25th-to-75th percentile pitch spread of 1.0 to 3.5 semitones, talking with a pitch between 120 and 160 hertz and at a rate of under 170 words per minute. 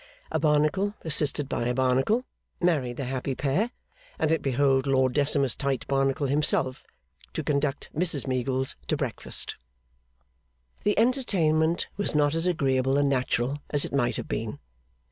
Yes: average, 3.2 semitones; medium, 140 Hz; average, 145 wpm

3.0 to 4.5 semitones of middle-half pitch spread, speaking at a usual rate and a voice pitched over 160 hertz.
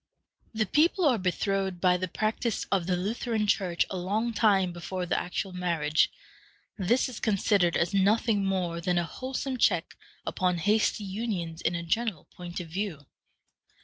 Yes: average, 3.6 semitones; average, 160 wpm; high, 190 Hz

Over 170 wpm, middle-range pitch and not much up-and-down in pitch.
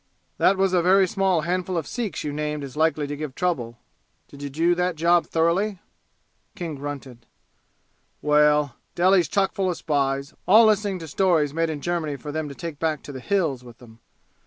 No: average, 190 wpm; medium, 160 Hz; average, 3.9 semitones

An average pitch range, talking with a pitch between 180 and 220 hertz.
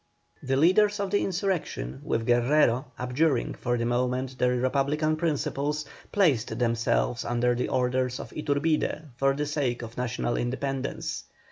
No: average, 3.7 semitones; low, 130 Hz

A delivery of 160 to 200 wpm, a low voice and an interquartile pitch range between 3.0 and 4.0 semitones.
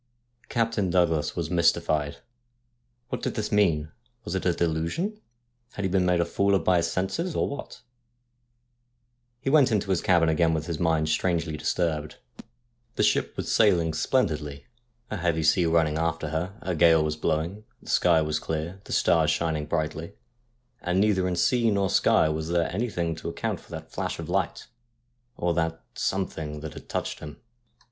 Yes: average, 180 wpm; very low, 85 Hz; average, 3.3 semitones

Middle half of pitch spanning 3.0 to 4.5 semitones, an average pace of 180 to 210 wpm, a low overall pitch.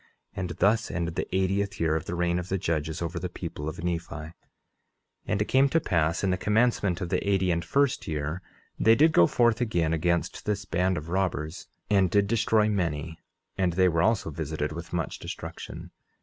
Yes: average, 3.6 semitones; average, 200 wpm; very low, 90 Hz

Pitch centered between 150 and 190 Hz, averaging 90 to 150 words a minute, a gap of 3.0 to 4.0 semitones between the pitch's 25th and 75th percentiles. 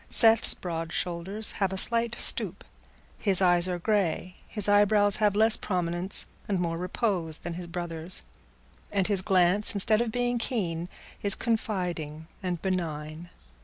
Yes: medium, 185 Hz; average, 145 wpm; average, 3.3 semitones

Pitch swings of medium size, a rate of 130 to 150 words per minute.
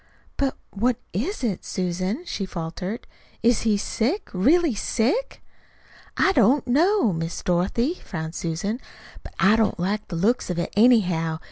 No: wide, 5.9 semitones; average, 145 wpm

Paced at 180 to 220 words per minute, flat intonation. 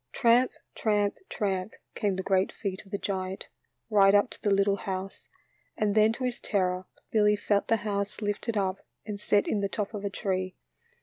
Yes: average, 190 wpm; narrow, 1.6 semitones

